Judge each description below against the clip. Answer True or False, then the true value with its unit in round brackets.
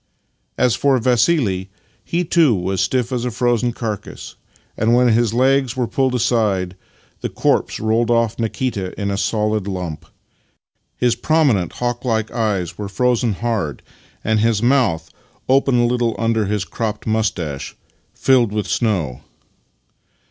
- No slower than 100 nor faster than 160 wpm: True (145 wpm)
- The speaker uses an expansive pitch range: False (3.5 semitones)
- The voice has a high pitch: False (115 Hz)